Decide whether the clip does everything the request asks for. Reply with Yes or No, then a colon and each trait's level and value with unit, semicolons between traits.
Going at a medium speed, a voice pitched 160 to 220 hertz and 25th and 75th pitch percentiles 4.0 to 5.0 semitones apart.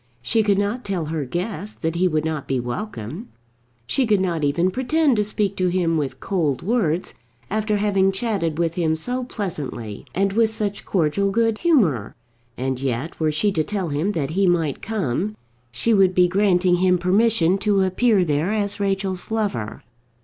Yes: average, 180 wpm; medium, 185 Hz; average, 4.7 semitones